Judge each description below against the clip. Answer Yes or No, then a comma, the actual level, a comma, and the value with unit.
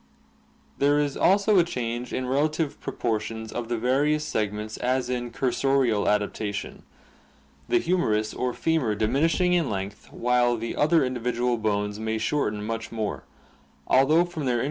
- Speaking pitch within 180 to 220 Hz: No, low, 125 Hz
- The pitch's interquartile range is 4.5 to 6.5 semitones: Yes, average, 4.9 semitones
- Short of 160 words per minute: No, average, 165 wpm